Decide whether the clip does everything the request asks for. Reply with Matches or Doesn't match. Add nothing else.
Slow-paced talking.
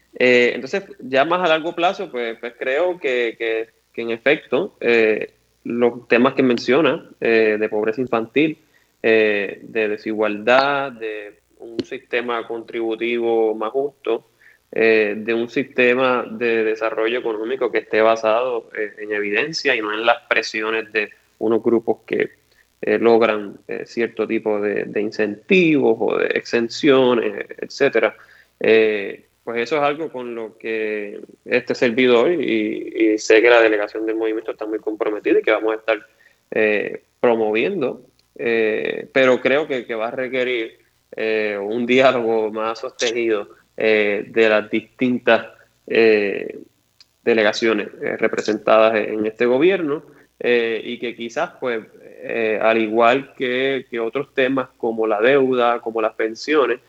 Doesn't match